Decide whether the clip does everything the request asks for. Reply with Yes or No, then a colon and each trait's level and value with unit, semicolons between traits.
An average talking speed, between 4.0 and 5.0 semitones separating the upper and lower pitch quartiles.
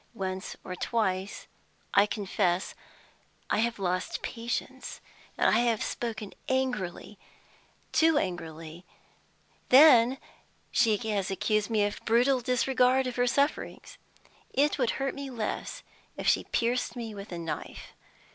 No: slow, 125 wpm; average, 4.5 semitones